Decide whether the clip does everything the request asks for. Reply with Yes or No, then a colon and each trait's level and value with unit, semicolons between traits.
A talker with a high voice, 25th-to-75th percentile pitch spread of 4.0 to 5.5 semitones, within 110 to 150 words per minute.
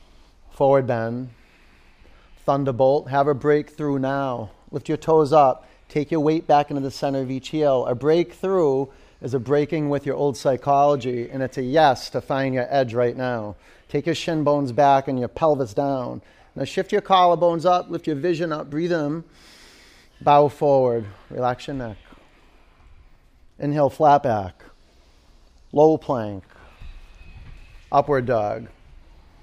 No: low, 135 Hz; average, 4.6 semitones; average, 145 wpm